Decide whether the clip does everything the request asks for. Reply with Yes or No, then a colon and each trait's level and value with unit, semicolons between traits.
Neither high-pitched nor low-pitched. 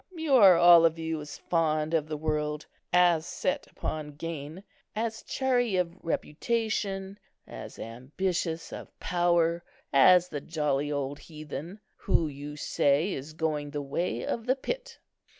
Yes: medium, 165 Hz